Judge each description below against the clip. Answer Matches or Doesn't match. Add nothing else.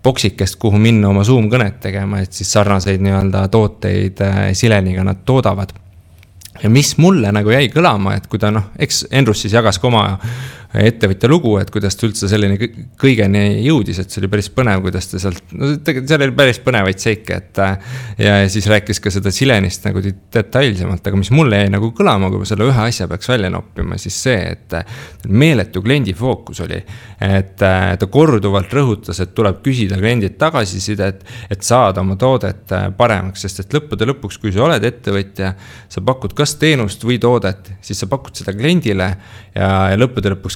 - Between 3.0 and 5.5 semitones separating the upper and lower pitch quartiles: Matches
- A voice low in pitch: Matches